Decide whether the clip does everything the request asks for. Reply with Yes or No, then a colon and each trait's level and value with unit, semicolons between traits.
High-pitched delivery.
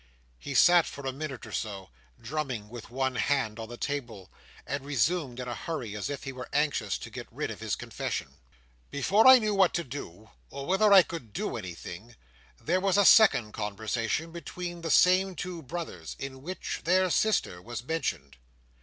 No: low, 135 Hz